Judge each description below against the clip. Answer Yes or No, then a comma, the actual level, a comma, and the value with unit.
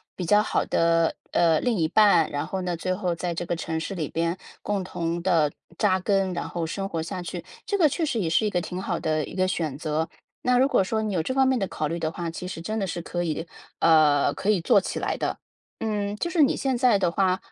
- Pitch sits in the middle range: Yes, medium, 180 Hz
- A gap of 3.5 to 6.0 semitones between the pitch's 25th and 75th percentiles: Yes, average, 3.9 semitones